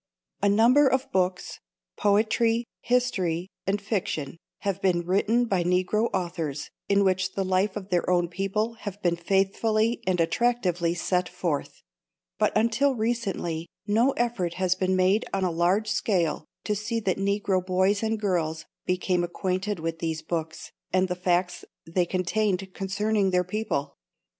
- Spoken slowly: No, average, 150 wpm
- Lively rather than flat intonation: No, average, 3.2 semitones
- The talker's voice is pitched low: No, high, 190 Hz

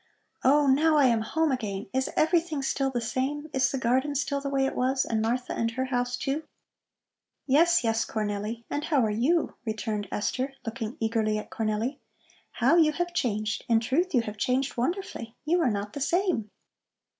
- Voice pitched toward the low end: No, very high, 255 Hz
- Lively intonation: No, average, 4.6 semitones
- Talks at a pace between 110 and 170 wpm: No, average, 185 wpm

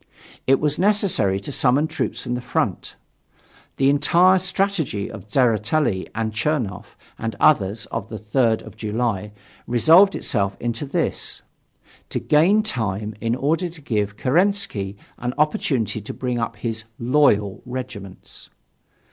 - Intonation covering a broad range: Yes, wide, 6.1 semitones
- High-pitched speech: No, low, 120 Hz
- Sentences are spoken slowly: Yes, slow, 130 wpm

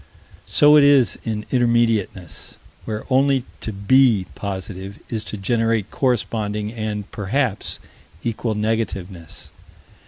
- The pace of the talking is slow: Yes, slow, 105 wpm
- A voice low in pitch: Yes, low, 110 Hz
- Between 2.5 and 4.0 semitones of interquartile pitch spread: Yes, average, 3.1 semitones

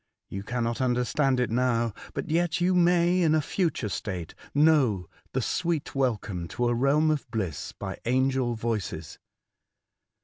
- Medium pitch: No, low, 125 Hz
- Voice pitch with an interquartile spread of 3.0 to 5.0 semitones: No, wide, 5.4 semitones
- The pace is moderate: Yes, average, 145 wpm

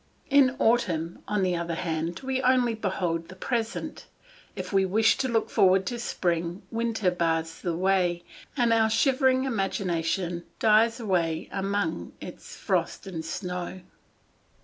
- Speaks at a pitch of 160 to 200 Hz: Yes, high, 190 Hz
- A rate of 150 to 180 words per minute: No, average, 140 wpm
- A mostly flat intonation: No, average, 4.9 semitones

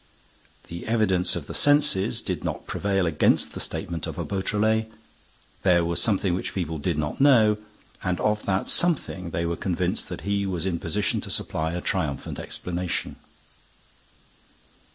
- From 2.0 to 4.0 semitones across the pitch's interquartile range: Yes, average, 3.4 semitones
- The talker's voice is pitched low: Yes, very low, 95 Hz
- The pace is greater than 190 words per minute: No, average, 155 wpm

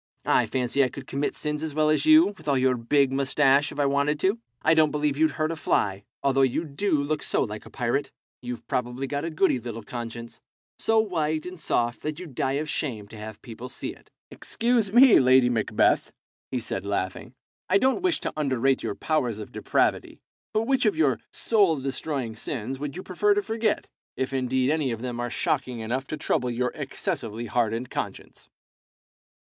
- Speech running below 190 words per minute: No, average, 195 wpm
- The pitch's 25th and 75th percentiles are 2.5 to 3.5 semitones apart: No, average, 4.4 semitones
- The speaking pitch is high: No, medium, 140 Hz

